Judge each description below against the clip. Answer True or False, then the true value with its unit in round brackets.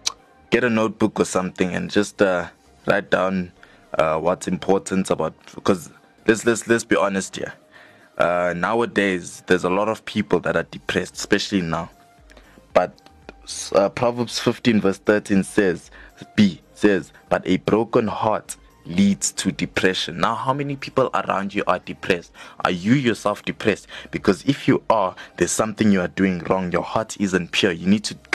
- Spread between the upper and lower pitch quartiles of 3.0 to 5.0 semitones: True (4.1 semitones)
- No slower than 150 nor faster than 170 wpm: True (165 wpm)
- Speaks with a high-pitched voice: False (105 Hz)